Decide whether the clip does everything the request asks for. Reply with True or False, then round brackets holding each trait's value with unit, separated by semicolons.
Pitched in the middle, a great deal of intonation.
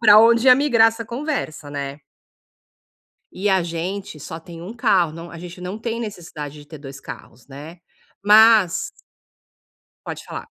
True (180 Hz; 6.0 semitones)